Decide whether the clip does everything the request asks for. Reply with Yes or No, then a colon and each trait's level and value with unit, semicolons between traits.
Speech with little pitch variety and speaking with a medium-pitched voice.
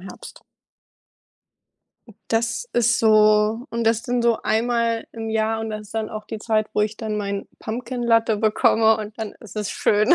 No: narrow, 1.3 semitones; high, 220 Hz